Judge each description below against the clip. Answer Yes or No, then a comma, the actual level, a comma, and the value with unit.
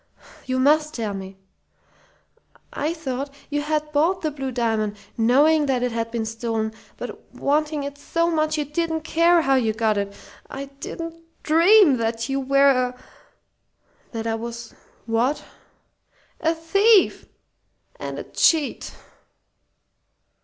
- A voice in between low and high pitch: No, very high, 275 Hz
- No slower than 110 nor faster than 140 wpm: Yes, slow, 135 wpm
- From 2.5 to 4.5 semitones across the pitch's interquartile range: No, average, 5.2 semitones